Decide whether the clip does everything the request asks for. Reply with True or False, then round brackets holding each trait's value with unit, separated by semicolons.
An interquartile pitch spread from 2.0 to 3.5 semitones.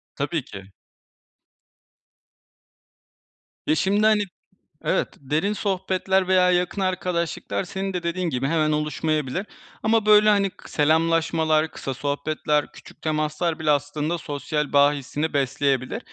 False (4.0 semitones)